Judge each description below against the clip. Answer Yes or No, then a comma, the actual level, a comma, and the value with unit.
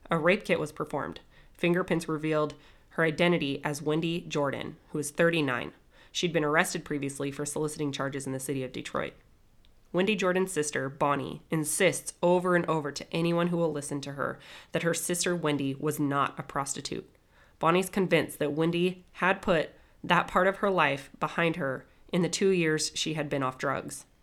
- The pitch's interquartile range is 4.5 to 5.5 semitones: No, average, 3.3 semitones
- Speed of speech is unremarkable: Yes, average, 180 wpm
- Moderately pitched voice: Yes, medium, 155 Hz